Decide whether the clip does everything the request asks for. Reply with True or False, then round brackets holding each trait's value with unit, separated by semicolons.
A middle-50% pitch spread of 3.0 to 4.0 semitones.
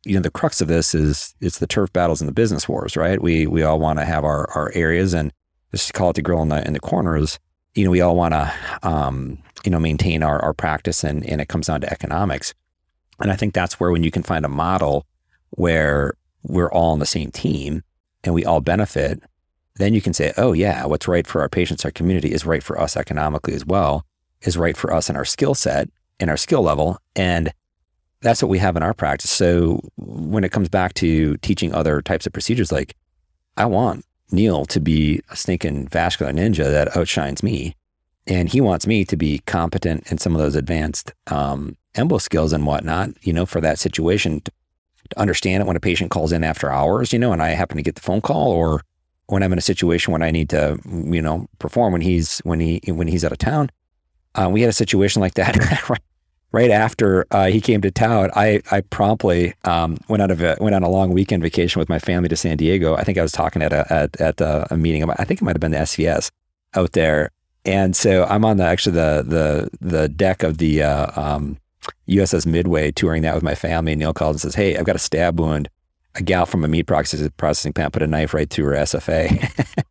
True (3.7 semitones)